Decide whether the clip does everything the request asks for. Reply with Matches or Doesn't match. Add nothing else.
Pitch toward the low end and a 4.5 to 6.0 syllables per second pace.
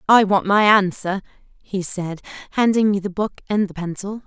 Doesn't match